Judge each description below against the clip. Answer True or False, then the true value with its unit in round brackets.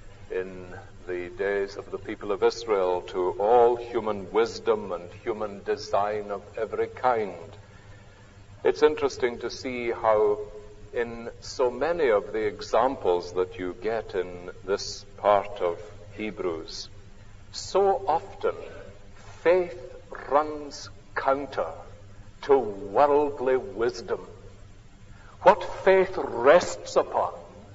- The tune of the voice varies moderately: False (8.4 semitones)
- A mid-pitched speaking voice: False (105 Hz)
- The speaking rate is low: True (105 wpm)